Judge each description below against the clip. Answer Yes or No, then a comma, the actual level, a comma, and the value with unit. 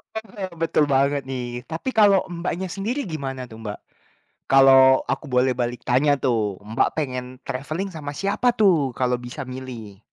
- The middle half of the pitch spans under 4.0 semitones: No, average, 5.0 semitones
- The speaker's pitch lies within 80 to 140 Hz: Yes, low, 135 Hz